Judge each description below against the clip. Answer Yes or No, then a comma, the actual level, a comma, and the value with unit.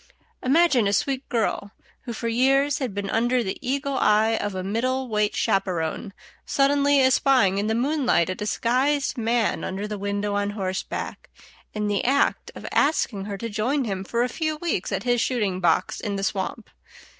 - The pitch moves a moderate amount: Yes, average, 4.6 semitones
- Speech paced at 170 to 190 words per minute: Yes, average, 180 wpm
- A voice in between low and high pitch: No, high, 225 Hz